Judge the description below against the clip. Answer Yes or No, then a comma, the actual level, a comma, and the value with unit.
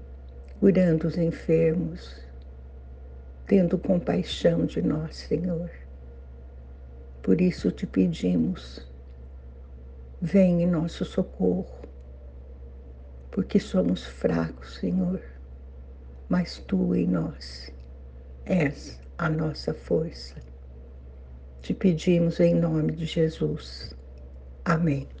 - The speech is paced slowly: Yes, slow, 85 wpm